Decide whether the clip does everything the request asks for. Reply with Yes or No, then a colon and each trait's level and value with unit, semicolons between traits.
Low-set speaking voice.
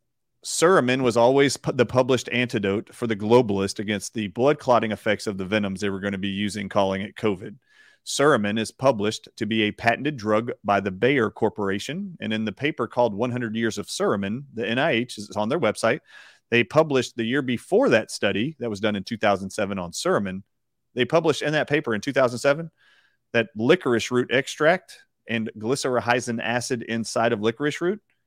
Yes: low, 115 Hz